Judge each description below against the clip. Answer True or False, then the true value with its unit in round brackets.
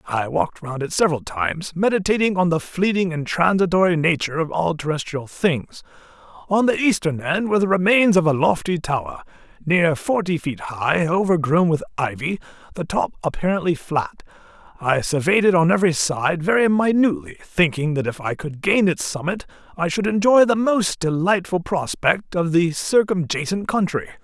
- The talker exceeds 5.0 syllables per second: True (5.2 syllables/s)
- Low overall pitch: False (170 Hz)